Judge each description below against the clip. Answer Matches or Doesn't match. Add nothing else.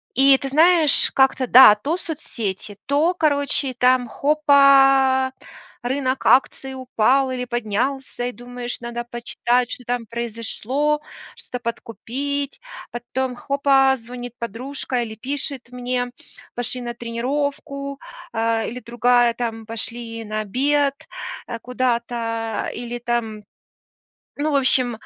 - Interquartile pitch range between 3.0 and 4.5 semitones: Doesn't match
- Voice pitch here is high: Matches